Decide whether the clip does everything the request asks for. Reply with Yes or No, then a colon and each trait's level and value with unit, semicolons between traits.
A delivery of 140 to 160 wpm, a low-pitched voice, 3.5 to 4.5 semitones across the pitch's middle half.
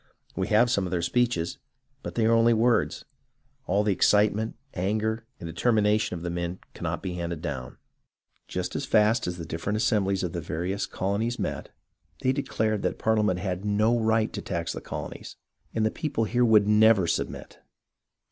No: average, 185 wpm; low, 105 Hz; average, 3.9 semitones